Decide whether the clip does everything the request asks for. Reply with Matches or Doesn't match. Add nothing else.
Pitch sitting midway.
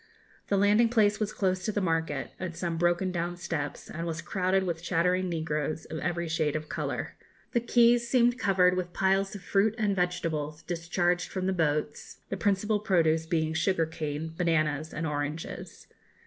Matches